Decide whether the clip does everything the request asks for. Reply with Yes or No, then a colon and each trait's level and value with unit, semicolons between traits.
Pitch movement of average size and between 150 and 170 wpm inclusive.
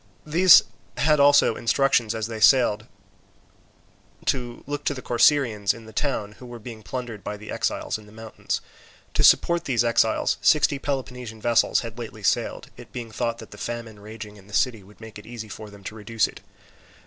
No: average, 3.0 semitones; average, 195 wpm